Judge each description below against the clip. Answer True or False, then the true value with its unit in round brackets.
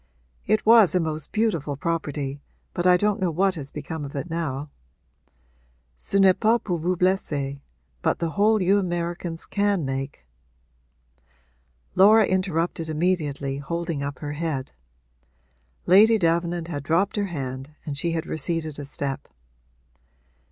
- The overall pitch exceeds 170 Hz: False (165 Hz)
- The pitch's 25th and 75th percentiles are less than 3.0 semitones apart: False (4.4 semitones)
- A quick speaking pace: False (145 wpm)